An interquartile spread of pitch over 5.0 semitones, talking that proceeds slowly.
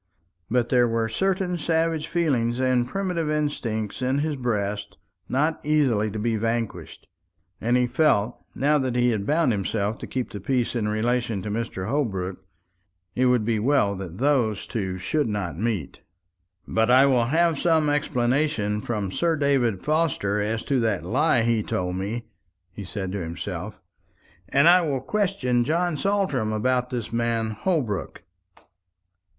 No: wide, 5.5 semitones; average, 155 wpm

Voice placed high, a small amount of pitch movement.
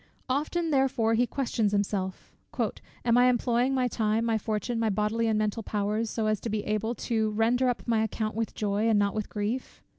Yes: high, 225 Hz; narrow, 2.3 semitones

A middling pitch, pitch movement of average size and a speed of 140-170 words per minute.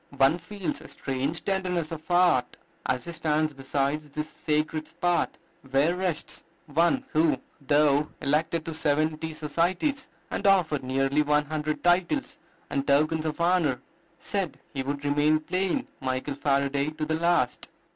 Yes: medium, 155 Hz; average, 3.1 semitones; average, 145 wpm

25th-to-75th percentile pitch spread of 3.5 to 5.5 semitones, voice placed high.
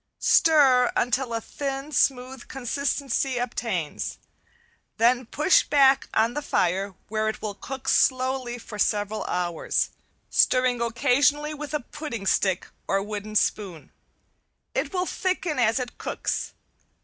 Yes: average, 4.1 semitones; high, 245 Hz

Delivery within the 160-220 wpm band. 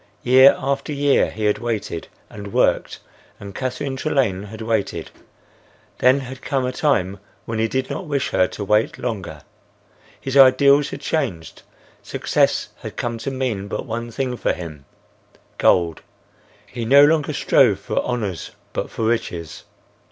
No: average, 150 wpm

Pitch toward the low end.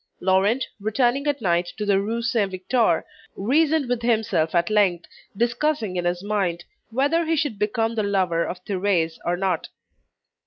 No: high, 205 Hz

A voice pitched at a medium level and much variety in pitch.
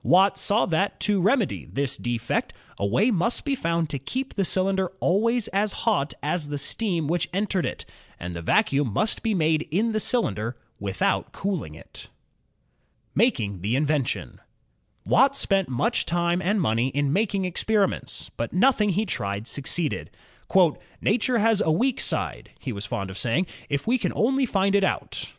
Yes: medium, 180 Hz; wide, 7.3 semitones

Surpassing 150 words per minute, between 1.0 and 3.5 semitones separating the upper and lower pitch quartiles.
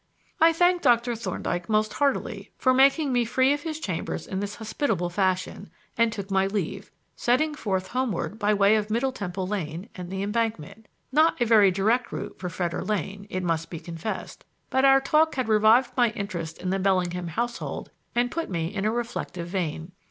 No: average, 190 wpm; average, 4.8 semitones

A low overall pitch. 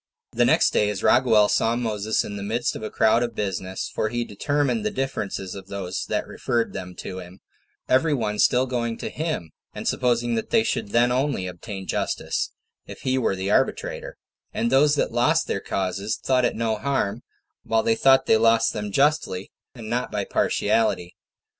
Yes: low, 115 Hz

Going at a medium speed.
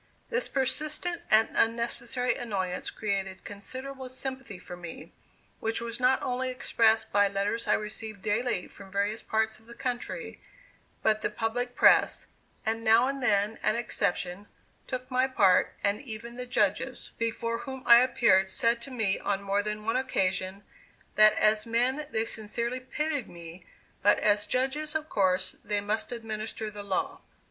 Yes: average, 155 wpm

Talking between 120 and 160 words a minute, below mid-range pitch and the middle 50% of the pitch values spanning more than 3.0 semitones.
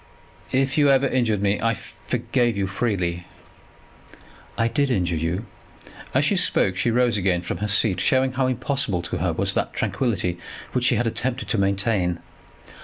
No: average, 175 wpm; low, 110 Hz; average, 5.1 semitones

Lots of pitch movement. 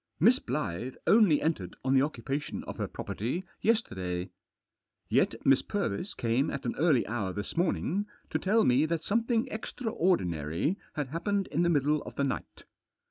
Yes: wide, 8.2 semitones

